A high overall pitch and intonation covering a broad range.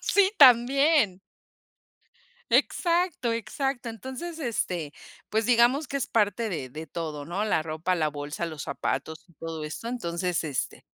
Yes: high, 210 Hz; wide, 8.3 semitones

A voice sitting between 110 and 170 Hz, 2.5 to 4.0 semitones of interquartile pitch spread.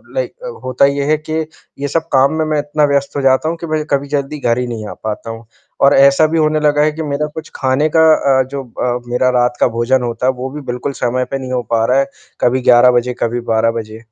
Yes: low, 135 Hz; average, 3.5 semitones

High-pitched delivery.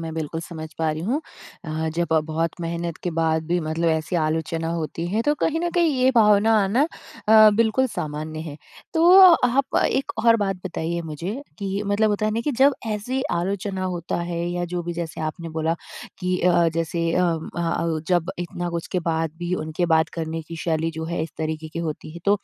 No: medium, 170 Hz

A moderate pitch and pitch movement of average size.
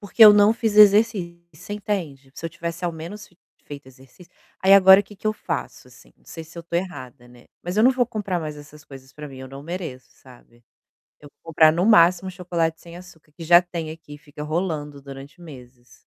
Yes: medium, 165 Hz; average, 4.5 semitones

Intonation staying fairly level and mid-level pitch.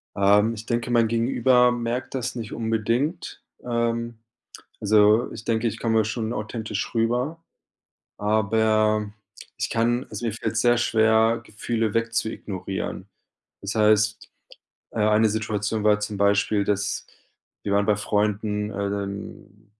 No: narrow, 1.9 semitones; low, 110 Hz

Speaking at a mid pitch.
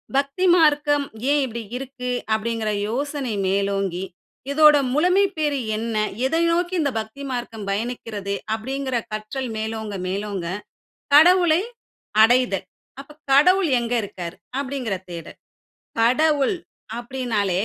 No: very high, 250 Hz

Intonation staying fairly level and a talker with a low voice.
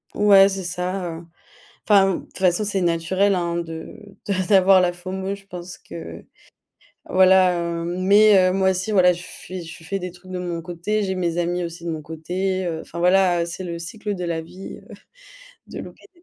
No: narrow, 1.9 semitones; medium, 185 Hz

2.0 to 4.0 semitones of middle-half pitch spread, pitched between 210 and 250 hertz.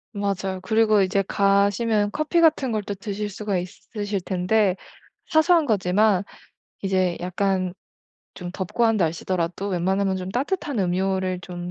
No: narrow, 2.6 semitones; high, 195 Hz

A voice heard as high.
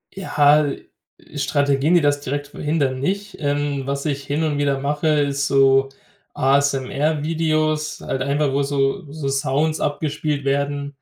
No: medium, 145 Hz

